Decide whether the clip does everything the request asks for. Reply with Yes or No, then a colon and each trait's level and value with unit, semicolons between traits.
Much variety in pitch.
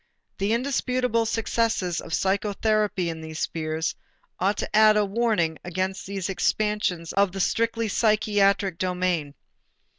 No: average, 3.4 semitones